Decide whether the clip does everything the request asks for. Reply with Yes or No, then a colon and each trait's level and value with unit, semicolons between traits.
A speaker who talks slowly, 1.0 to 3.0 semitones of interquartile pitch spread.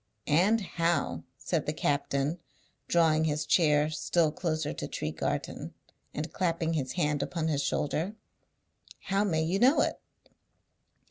Yes: slow, 130 wpm; average, 2.7 semitones